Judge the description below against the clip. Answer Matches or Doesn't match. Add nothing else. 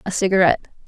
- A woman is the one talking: Matches